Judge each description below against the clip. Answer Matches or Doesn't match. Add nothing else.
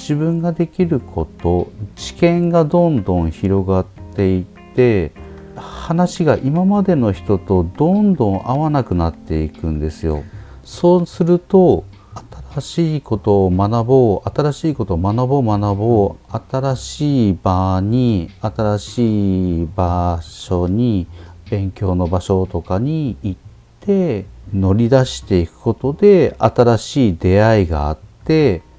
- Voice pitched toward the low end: Matches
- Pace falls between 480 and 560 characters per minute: Doesn't match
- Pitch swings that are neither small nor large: Doesn't match